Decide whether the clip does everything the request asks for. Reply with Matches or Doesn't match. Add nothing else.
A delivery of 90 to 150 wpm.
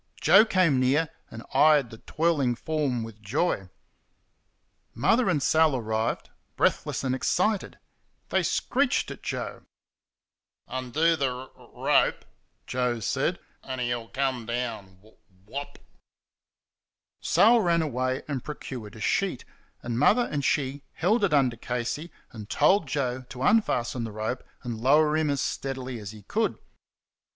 Matches